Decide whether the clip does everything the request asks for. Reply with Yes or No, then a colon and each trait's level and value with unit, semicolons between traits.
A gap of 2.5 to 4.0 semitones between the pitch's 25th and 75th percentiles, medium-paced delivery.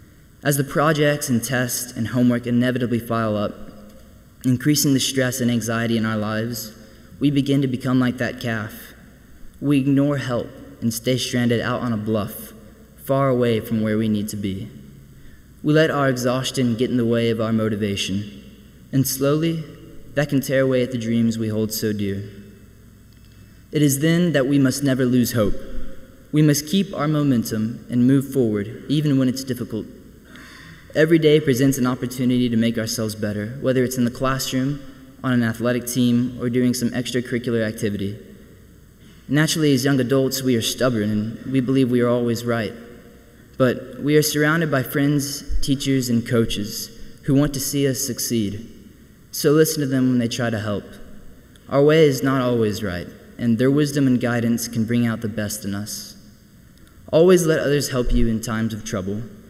Yes: average, 3.3 semitones; average, 175 wpm